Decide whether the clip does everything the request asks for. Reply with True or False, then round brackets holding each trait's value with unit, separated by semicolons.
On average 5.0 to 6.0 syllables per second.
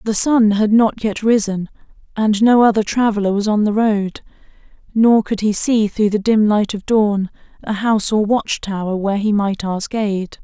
False (4.7 syllables/s)